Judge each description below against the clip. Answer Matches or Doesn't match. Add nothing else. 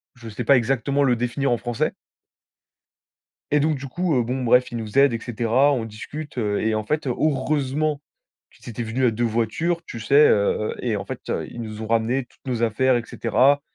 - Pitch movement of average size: Matches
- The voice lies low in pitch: Matches